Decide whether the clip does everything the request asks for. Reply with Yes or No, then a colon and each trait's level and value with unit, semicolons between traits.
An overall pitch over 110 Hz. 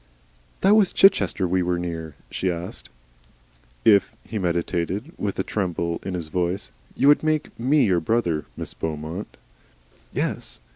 No: very low, 90 Hz